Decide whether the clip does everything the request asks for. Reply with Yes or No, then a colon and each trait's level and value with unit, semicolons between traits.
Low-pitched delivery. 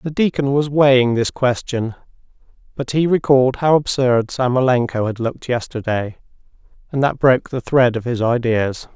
Yes: low, 130 Hz